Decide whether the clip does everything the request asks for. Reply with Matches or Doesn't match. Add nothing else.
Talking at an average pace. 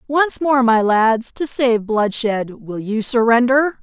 Matches